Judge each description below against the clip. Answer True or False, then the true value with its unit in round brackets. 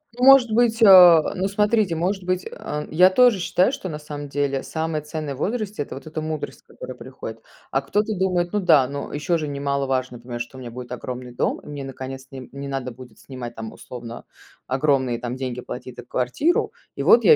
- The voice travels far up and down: True (6.1 semitones)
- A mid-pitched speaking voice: True (145 Hz)